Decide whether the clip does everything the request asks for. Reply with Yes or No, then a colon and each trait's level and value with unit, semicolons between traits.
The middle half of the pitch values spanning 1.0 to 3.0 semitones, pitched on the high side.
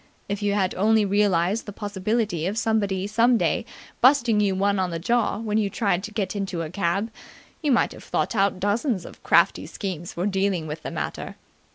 Yes: average, 2.7 semitones; high, 200 Hz